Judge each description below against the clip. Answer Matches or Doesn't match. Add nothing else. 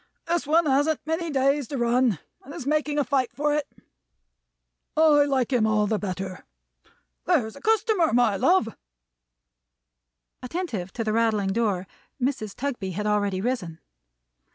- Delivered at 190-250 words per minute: Doesn't match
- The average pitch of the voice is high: Matches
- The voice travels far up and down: Matches